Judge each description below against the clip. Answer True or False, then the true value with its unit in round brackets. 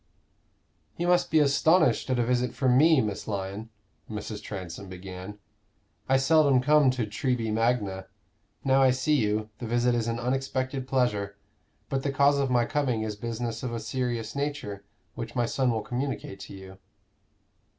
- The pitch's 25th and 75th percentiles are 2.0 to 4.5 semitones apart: True (3.8 semitones)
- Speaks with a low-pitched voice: True (120 Hz)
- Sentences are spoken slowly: False (165 wpm)